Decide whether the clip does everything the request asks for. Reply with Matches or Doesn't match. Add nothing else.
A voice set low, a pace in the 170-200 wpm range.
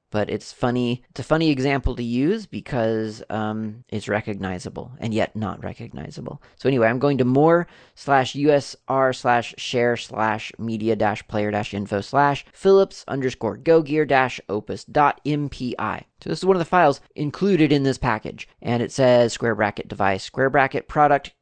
Matches